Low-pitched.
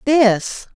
No: very high, 250 Hz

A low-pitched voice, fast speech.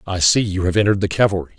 Yes: very low, 95 Hz; fast, 265 wpm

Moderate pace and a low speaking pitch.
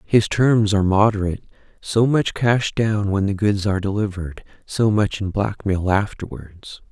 Yes: average, 155 wpm; low, 100 Hz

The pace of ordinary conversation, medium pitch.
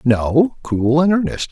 Yes: average, 160 wpm; medium, 150 Hz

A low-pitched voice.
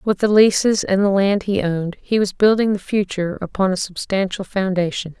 No: high, 195 Hz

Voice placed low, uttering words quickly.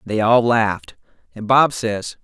No: low, 115 Hz; average, 160 wpm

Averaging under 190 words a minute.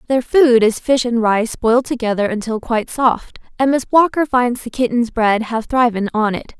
No: average, 200 wpm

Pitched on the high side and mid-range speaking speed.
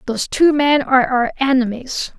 Yes: very high, 260 Hz; average, 165 wpm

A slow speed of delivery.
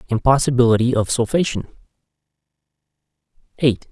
Yes: slow, 60 wpm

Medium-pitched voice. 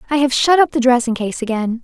No: very high, 255 Hz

